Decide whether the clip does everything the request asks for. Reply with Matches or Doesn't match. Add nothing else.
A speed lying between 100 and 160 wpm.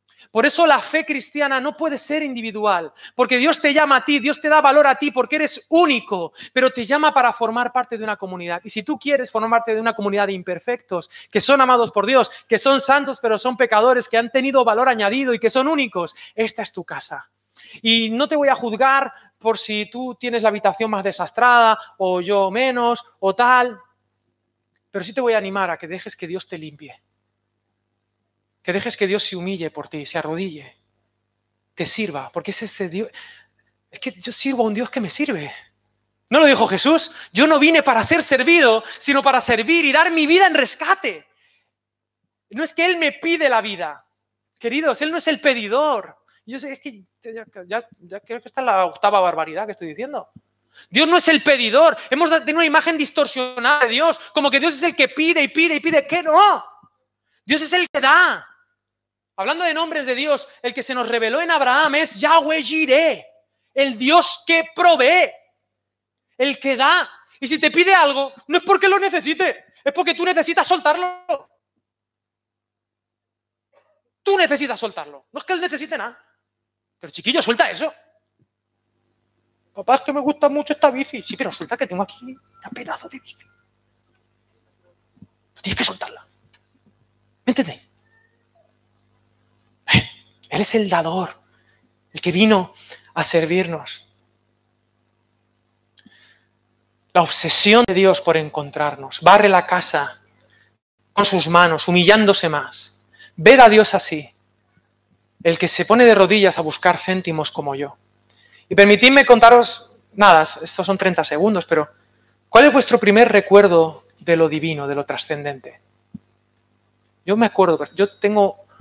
Doesn't match